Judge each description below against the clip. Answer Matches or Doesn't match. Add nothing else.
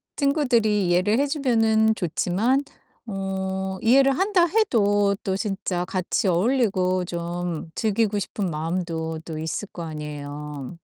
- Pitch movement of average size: Matches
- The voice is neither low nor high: Doesn't match